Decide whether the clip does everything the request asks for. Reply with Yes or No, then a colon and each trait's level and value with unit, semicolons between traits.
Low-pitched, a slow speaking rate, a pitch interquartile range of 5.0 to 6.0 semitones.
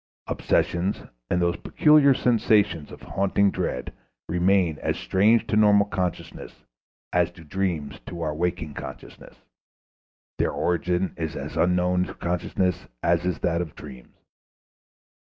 No: very low, 90 Hz; slow, 130 wpm; average, 2.8 semitones